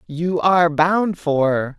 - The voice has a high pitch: No, medium, 165 Hz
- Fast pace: No, slow, 135 wpm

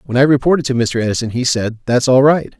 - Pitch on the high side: No, low, 130 Hz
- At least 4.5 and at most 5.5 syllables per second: No, 6.3 syllables/s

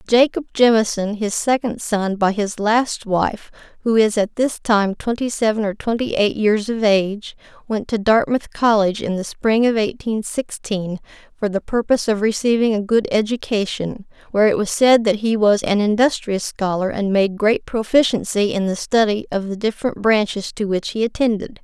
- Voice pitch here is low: No, high, 215 Hz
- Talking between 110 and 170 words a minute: No, average, 180 wpm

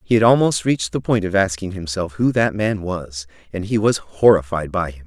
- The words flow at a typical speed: No, fast, 225 wpm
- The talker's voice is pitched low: Yes, low, 100 Hz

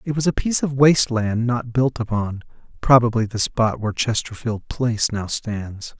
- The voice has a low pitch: Yes, low, 120 Hz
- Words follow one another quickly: No, average, 170 wpm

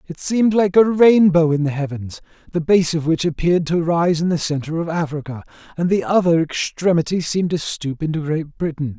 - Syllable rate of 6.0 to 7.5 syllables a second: No, 5.5 syllables/s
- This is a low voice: No, medium, 165 Hz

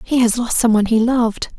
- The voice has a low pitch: No, high, 235 Hz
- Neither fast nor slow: No, fast, 225 wpm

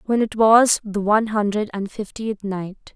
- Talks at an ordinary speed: Yes, average, 185 wpm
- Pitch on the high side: Yes, high, 210 Hz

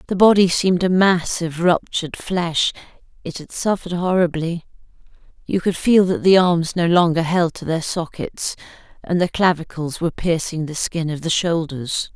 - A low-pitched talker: No, medium, 170 Hz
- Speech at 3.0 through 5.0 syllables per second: Yes, 4.8 syllables/s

